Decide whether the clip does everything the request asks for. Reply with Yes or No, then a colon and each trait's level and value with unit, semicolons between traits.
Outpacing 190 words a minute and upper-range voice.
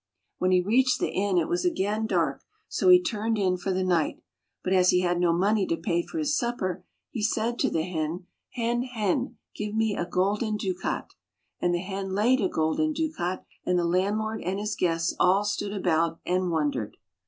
Yes: average, 200 wpm; high, 195 Hz